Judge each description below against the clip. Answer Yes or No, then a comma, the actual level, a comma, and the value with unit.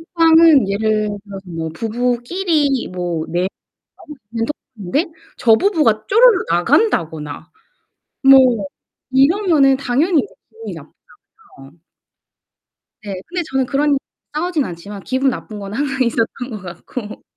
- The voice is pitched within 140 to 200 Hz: No, very high, 250 Hz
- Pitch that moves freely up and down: Yes, wide, 7.2 semitones